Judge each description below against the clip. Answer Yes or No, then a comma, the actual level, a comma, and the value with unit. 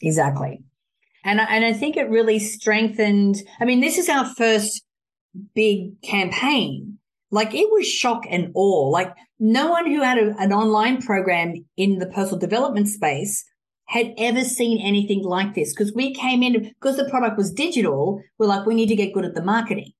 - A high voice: Yes, high, 215 Hz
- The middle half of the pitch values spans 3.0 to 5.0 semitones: Yes, average, 3.4 semitones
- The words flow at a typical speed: Yes, average, 185 wpm